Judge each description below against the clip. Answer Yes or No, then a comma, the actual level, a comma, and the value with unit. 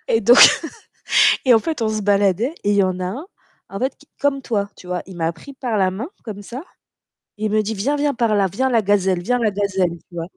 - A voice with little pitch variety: No, average, 4.3 semitones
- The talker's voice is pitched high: Yes, high, 210 Hz